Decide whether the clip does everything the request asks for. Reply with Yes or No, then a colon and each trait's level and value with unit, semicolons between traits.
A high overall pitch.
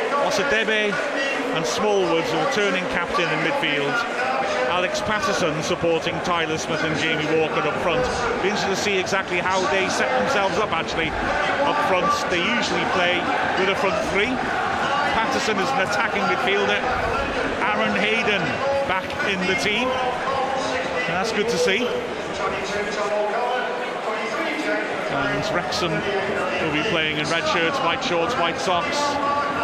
Yes: high, 205 Hz